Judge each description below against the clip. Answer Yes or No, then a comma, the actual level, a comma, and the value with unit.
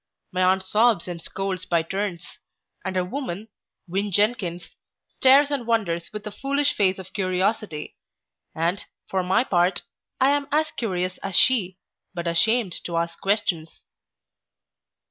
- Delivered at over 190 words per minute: No, average, 145 wpm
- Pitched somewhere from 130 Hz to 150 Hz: No, high, 190 Hz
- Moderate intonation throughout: Yes, average, 4.1 semitones